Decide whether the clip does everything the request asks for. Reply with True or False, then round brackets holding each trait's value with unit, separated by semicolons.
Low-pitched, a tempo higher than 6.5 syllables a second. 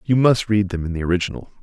True (100 Hz; 6.9 syllables/s)